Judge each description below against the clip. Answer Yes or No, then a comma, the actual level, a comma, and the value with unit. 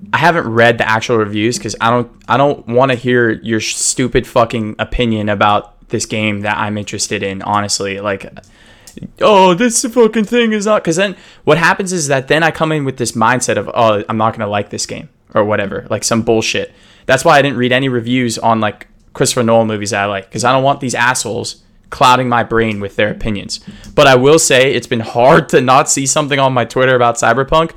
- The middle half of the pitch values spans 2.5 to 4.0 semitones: No, average, 4.5 semitones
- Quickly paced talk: Yes, fast, 220 wpm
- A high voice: No, low, 120 Hz